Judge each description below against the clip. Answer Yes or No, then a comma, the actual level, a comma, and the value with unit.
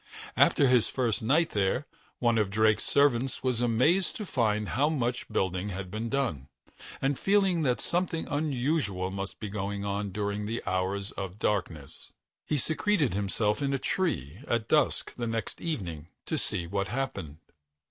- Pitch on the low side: Yes, low, 115 Hz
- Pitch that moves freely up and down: Yes, wide, 5.9 semitones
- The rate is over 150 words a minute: Yes, average, 160 wpm